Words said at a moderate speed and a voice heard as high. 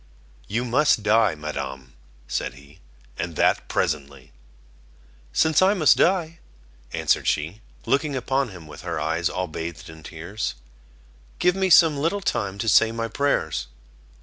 No: average, 145 wpm; low, 100 Hz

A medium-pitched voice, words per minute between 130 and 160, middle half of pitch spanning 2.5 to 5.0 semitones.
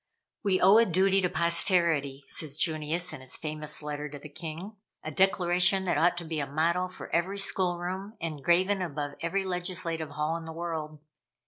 No: medium, 170 Hz; average, 185 wpm; average, 3.2 semitones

